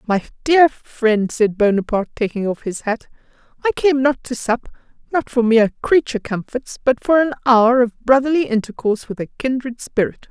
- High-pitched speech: Yes, high, 245 Hz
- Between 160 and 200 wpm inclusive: Yes, average, 175 wpm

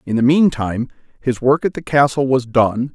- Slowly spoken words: No, fast, 205 wpm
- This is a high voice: No, low, 130 Hz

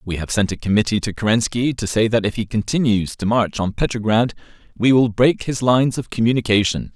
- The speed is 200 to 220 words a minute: Yes, fast, 205 wpm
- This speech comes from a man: Yes, male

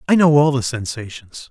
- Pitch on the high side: No, low, 130 Hz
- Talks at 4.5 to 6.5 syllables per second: Yes, 5.2 syllables/s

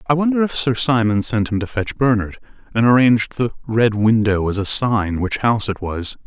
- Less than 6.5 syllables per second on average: Yes, 5.3 syllables/s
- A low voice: Yes, low, 115 Hz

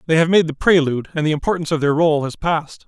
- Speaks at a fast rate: Yes, fast, 270 wpm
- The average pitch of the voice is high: No, medium, 160 Hz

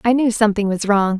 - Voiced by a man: No, female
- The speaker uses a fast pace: Yes, fast, 250 wpm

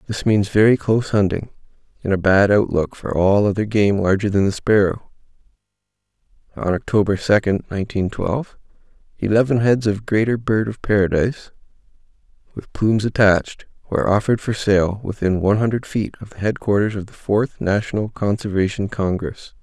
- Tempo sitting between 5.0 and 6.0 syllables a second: Yes, 5.5 syllables/s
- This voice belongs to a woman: No, male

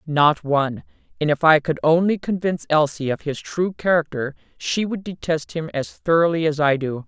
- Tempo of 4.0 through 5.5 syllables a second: Yes, 5.1 syllables/s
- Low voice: No, medium, 160 Hz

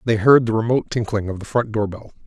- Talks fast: Yes, fast, 265 wpm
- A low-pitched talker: Yes, low, 110 Hz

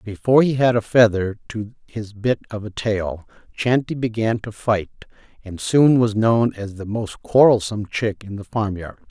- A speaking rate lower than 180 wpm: No, average, 185 wpm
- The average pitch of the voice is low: Yes, low, 110 Hz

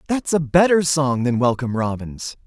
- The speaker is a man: Yes, male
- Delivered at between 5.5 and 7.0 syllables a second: No, 5.0 syllables/s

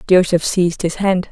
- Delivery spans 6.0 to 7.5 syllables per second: No, 5.3 syllables/s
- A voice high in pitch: No, medium, 180 Hz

